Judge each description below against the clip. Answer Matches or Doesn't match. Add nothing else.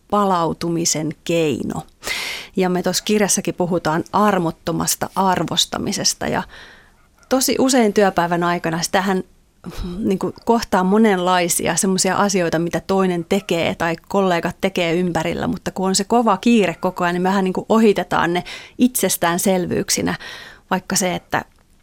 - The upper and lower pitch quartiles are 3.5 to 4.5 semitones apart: Doesn't match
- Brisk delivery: Doesn't match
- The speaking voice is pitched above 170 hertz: Matches